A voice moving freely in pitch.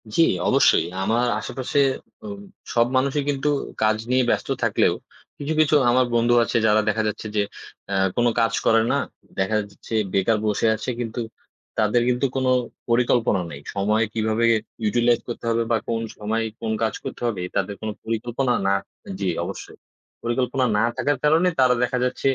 No: average, 2.7 semitones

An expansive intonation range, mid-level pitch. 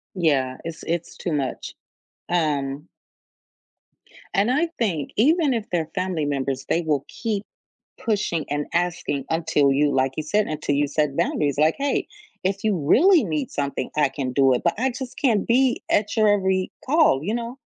Yes: wide, 6.9 semitones; medium, 165 Hz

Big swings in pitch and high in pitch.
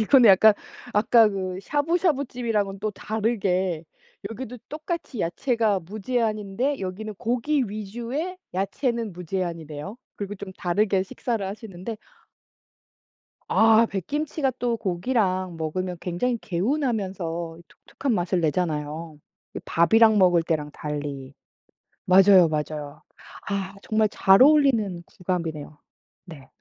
No: average, 5.0 semitones; high, 195 Hz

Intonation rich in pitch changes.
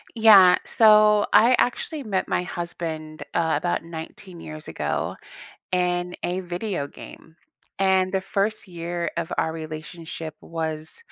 No: average, 3.2 semitones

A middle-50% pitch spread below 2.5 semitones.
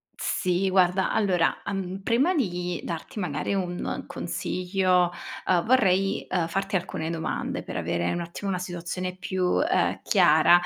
Yes: narrow, 1.8 semitones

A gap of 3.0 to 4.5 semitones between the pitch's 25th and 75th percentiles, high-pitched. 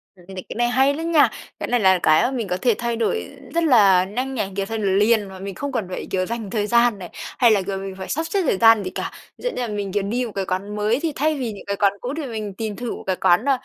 Yes: average, 4.1 semitones; high, 215 Hz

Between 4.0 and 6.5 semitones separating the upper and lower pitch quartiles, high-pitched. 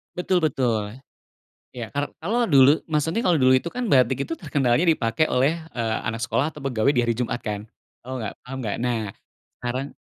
No: average, 4.6 semitones; low, 130 Hz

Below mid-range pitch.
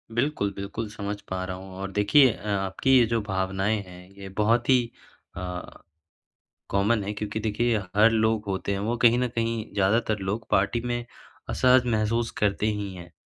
Yes: low, 105 Hz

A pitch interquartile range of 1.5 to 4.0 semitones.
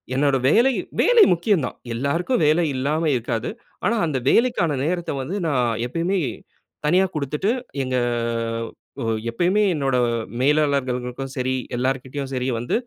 No: average, 5.1 semitones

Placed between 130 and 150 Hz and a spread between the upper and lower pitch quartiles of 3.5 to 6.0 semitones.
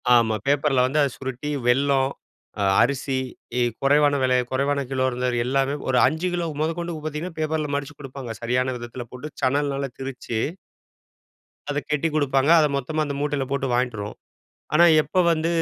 No: medium, 140 Hz; average, 2.7 semitones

